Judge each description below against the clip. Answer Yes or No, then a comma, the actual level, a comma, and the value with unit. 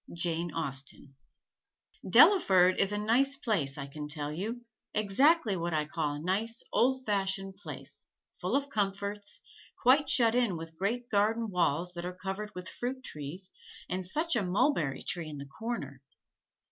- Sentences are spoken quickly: No, average, 160 wpm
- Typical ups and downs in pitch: No, wide, 5.8 semitones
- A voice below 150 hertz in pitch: No, high, 195 Hz